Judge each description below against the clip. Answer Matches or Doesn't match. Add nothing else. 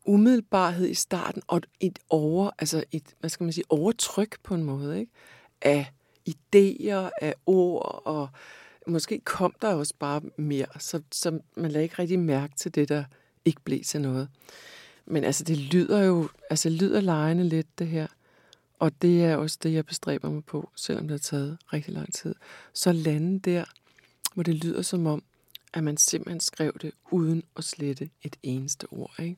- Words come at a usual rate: Matches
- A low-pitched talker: Doesn't match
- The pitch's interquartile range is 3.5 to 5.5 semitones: Doesn't match